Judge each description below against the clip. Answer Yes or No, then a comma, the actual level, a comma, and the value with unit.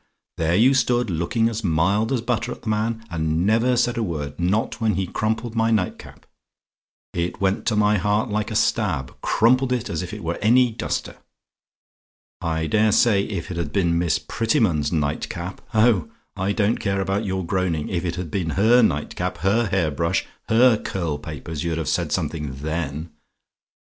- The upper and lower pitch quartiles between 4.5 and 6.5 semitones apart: Yes, average, 5.1 semitones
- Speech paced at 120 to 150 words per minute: No, average, 190 wpm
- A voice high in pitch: No, very low, 95 Hz